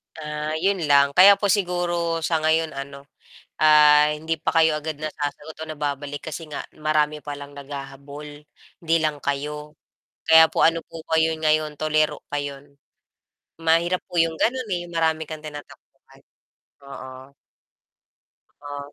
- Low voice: No, medium, 155 Hz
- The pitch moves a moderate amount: No, narrow, 1.9 semitones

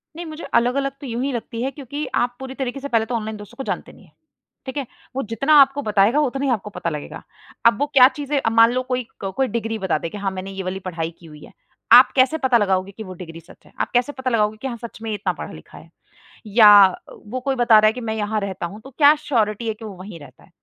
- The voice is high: Yes, high, 230 Hz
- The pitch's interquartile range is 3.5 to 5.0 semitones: Yes, average, 4.4 semitones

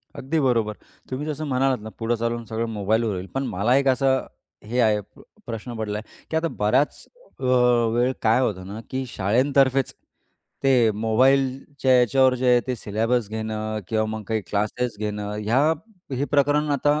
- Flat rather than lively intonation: No, average, 3.5 semitones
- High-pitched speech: No, low, 120 Hz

